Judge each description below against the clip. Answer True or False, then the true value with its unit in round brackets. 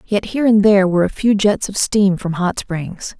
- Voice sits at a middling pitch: False (195 Hz)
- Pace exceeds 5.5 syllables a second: False (5.2 syllables/s)